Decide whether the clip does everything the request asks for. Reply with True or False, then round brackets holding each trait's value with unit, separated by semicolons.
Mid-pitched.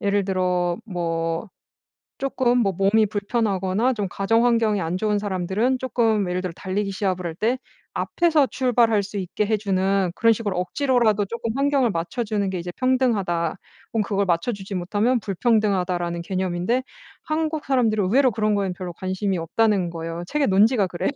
False (205 Hz)